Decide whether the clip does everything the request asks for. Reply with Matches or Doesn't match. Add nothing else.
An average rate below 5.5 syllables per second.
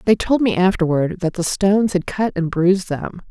Matches